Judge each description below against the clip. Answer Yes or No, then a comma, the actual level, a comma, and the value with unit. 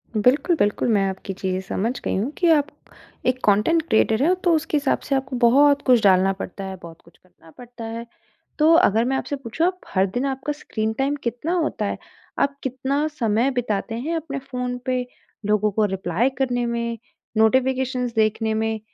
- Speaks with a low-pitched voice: No, high, 245 Hz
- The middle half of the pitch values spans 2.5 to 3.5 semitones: No, average, 4.2 semitones